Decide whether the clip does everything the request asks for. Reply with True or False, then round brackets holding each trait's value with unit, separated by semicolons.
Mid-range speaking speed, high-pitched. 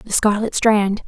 True (170 wpm; 210 Hz)